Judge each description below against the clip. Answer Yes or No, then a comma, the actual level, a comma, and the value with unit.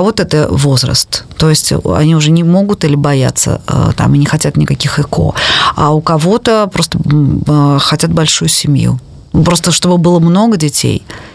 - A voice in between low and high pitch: Yes, medium, 155 Hz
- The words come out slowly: No, average, 155 wpm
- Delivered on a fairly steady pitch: No, average, 3.4 semitones